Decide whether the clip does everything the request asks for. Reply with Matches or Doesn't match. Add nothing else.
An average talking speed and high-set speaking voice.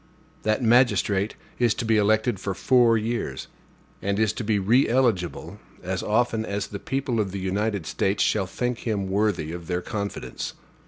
Doesn't match